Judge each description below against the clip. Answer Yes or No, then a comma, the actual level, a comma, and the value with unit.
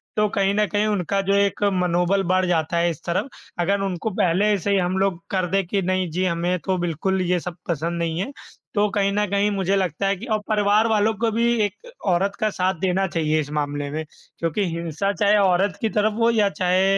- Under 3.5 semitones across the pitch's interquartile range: Yes, average, 2.8 semitones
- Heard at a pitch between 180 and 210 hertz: Yes, high, 190 Hz